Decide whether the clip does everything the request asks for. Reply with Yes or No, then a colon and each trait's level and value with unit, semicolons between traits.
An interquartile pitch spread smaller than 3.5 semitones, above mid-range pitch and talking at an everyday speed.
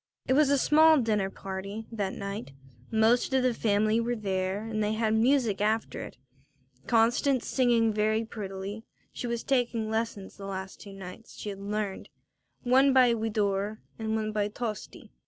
Yes: narrow, 2.6 semitones; high, 220 Hz; average, 165 wpm